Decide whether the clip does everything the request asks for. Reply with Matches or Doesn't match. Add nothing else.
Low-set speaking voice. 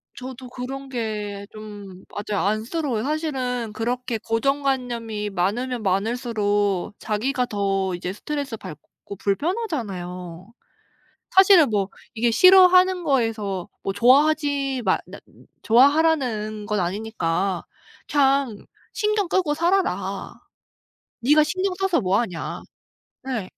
Doesn't match